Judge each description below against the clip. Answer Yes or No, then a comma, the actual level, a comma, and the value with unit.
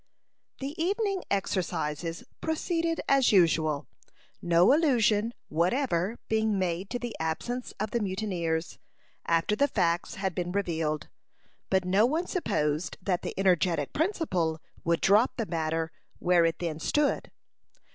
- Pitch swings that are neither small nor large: No, wide, 6.4 semitones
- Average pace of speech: No, slow, 130 wpm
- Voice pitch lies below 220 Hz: Yes, high, 190 Hz